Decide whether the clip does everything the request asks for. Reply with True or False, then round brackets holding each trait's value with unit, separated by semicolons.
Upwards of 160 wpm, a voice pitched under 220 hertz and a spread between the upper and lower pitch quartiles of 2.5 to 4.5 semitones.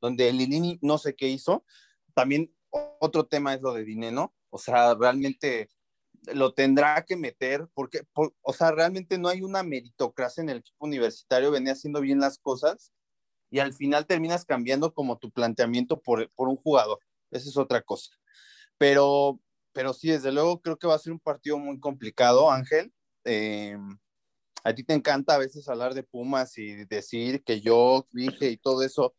True (180 wpm; 140 Hz; 4.0 semitones)